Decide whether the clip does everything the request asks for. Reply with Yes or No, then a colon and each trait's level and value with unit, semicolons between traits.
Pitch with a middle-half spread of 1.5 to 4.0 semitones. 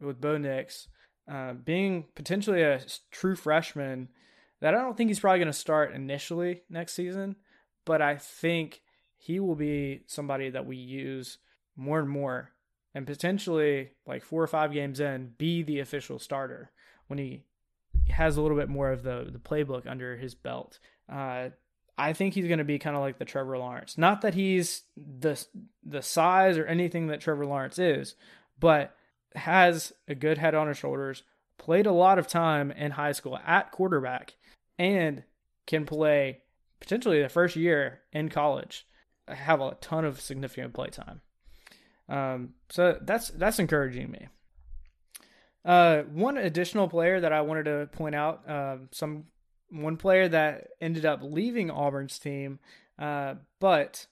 Yes: average, 3.7 semitones